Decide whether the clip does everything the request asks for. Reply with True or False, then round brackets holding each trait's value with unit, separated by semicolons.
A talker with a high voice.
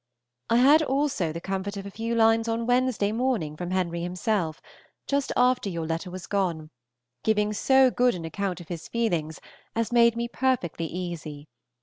True (200 Hz)